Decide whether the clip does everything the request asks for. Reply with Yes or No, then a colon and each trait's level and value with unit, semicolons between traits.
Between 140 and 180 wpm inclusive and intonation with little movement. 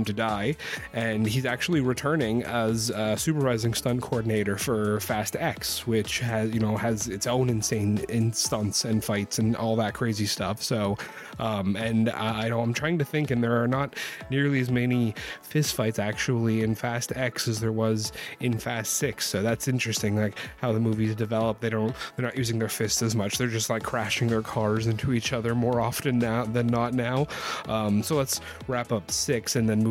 No: average, 200 wpm; narrow, 2.0 semitones